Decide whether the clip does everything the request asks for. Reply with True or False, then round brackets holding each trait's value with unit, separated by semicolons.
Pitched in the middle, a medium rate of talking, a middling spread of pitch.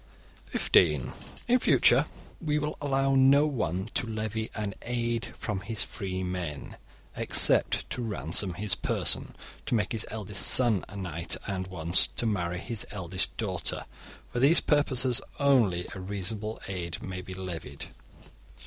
False (105 Hz; 145 wpm; 4.7 semitones)